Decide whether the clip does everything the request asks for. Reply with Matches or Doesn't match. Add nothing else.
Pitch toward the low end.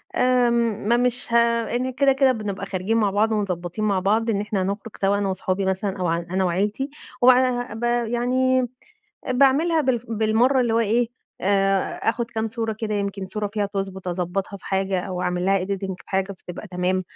Doesn't match